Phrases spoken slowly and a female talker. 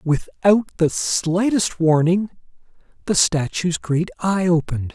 No: slow, 110 wpm; male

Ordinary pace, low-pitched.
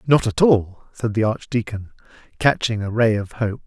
Yes: average, 180 wpm; low, 115 Hz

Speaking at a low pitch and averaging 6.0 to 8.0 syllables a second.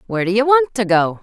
No: high, 225 Hz; 6.5 syllables/s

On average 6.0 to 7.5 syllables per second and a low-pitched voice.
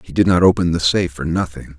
Yes: 6.5 syllables/s; very low, 85 Hz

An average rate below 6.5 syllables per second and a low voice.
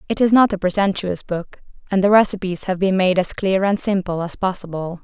No: 5.5 syllables/s; high, 190 Hz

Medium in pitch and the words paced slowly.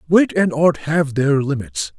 No: medium, 145 Hz; average, 180 wpm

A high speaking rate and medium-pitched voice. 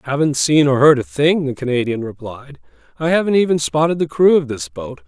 Yes: fast, 215 wpm; medium, 150 Hz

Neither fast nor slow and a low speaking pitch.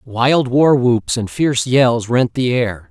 Yes: average, 185 wpm; low, 125 Hz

